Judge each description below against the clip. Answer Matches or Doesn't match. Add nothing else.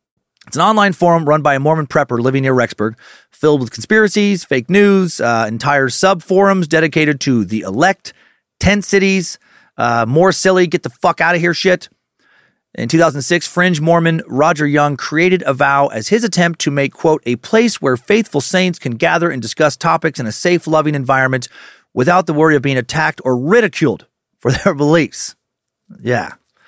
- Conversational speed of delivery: Matches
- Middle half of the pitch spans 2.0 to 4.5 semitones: Doesn't match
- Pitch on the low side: Doesn't match